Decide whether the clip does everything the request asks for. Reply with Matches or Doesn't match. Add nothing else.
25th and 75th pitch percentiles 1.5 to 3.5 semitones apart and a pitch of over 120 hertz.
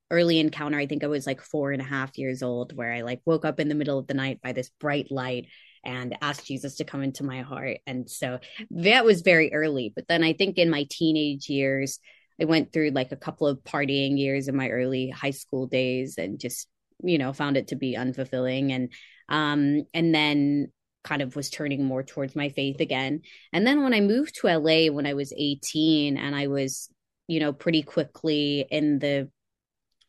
Matches